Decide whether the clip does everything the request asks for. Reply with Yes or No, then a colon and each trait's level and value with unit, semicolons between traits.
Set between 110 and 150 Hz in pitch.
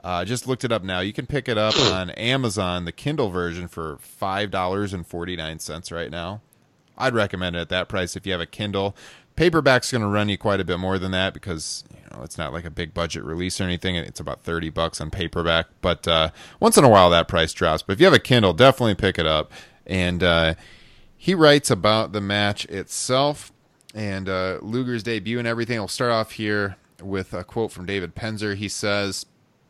No: very low, 95 Hz